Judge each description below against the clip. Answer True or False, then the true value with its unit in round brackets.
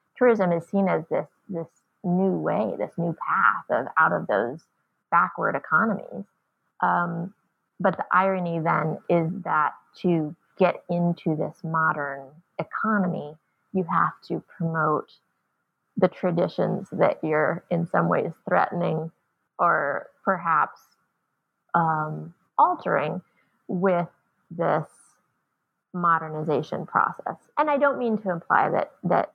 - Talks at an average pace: False (120 wpm)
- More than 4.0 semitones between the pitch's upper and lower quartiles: False (2.8 semitones)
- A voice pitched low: False (175 Hz)